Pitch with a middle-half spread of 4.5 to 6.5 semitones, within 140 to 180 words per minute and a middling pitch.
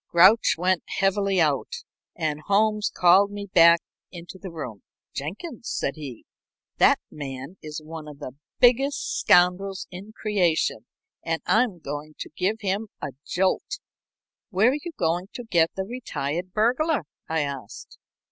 Yes: average, 5.2 semitones; average, 145 wpm; medium, 180 Hz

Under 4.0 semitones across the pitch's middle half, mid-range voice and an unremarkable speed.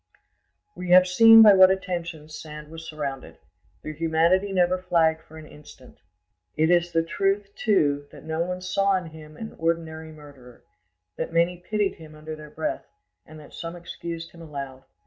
Yes: average, 2.8 semitones; medium, 165 Hz; average, 170 wpm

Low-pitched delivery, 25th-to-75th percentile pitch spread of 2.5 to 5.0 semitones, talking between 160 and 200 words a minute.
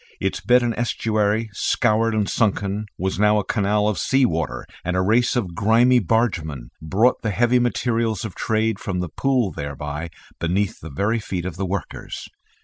Yes: low, 105 Hz; average, 3.7 semitones; average, 175 wpm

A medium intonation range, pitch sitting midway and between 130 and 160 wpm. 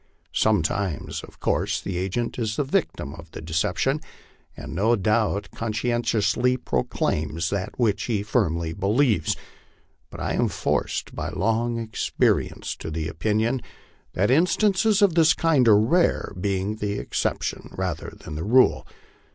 No: average, 4.9 semitones; low, 110 Hz; average, 145 wpm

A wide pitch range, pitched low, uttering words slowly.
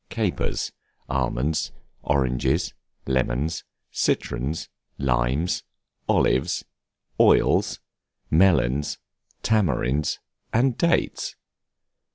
No: average, 4.7 semitones; very low, 70 Hz; slow, 60 wpm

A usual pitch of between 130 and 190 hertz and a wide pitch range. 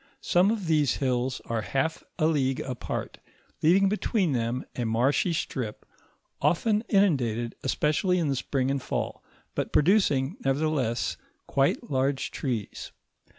No: medium, 140 Hz; average, 4.7 semitones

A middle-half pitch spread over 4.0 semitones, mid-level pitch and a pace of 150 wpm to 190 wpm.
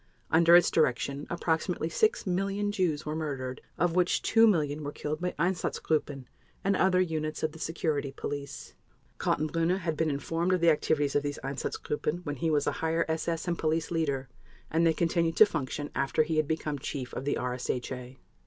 No: average, 2.9 semitones; medium, 160 Hz; average, 180 wpm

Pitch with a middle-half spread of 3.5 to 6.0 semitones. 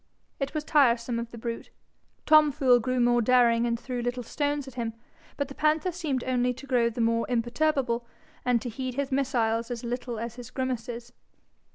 No: narrow, 2.6 semitones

